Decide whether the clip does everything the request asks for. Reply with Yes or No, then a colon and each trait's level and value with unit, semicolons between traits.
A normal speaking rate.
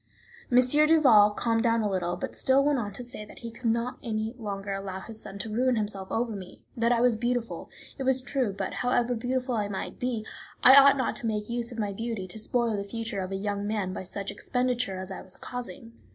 No: fast, 235 wpm